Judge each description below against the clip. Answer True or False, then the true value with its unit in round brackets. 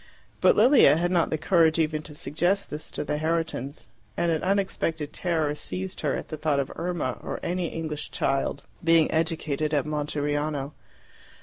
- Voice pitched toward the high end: False (155 Hz)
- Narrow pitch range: True (2.2 semitones)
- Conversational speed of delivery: True (170 wpm)